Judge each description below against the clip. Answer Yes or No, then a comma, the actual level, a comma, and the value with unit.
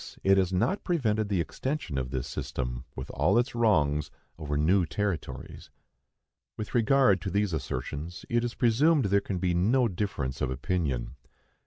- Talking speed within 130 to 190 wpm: Yes, average, 160 wpm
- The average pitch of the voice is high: No, very low, 95 Hz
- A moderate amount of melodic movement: No, wide, 7.7 semitones